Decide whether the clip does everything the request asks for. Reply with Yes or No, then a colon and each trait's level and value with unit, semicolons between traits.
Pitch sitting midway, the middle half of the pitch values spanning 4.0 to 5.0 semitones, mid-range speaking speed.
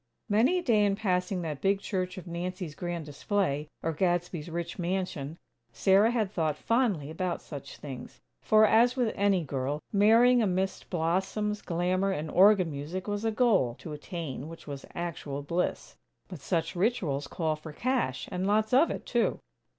Yes: medium, 180 Hz; average, 4.6 semitones; average, 165 wpm